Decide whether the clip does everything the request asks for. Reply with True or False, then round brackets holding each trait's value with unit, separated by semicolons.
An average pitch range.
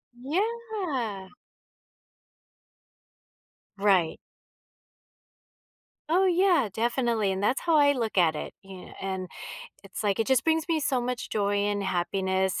False (7.6 semitones)